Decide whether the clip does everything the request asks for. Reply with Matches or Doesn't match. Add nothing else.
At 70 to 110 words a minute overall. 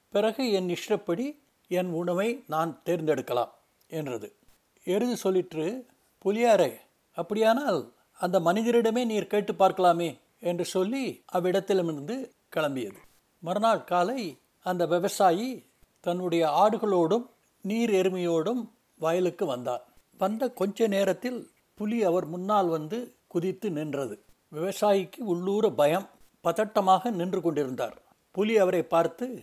Matches